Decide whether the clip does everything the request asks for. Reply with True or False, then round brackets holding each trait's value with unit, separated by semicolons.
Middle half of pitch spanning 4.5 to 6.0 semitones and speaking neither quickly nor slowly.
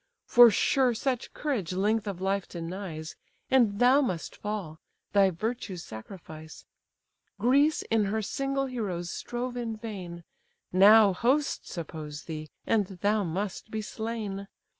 False (4.9 semitones; 130 wpm)